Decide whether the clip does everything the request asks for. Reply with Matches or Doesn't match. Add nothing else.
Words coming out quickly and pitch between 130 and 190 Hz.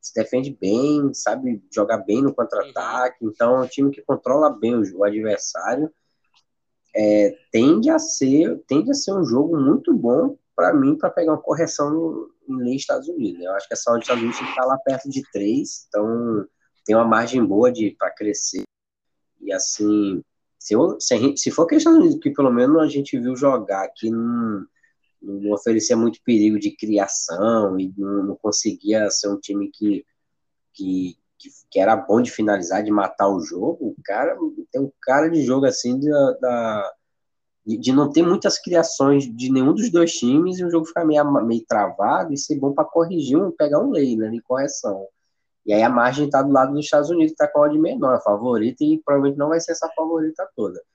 Matches